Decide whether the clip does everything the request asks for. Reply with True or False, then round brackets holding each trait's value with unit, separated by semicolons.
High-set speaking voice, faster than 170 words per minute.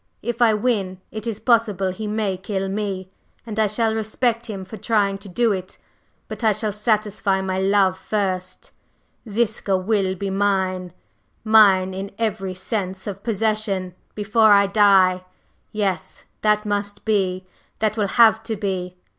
False (205 Hz; 155 wpm)